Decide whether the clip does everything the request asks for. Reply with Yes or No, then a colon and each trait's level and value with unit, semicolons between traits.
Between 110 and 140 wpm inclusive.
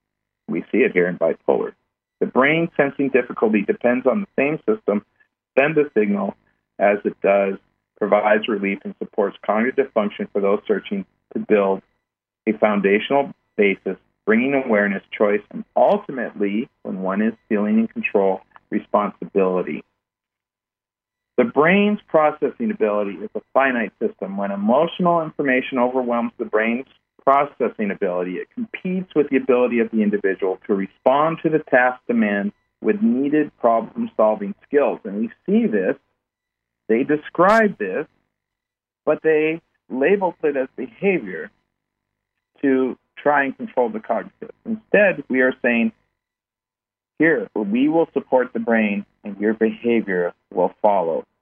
Yes: slow, 135 wpm